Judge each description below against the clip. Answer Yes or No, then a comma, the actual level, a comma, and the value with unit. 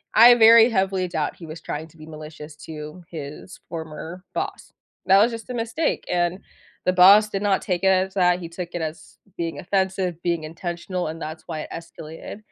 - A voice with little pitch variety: No, average, 3.1 semitones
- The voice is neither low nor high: Yes, medium, 175 Hz